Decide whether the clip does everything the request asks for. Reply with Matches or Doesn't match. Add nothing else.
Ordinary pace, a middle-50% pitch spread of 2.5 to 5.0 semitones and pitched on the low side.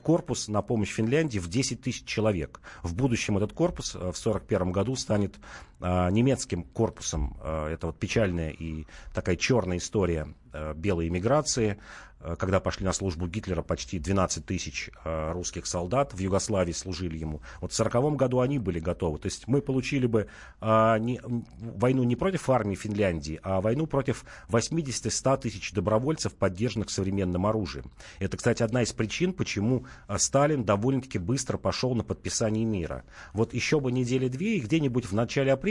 Doesn't match